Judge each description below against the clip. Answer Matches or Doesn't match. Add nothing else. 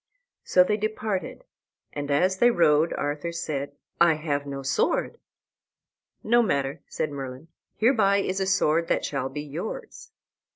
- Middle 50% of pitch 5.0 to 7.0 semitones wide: Matches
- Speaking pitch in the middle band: Matches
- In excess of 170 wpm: Doesn't match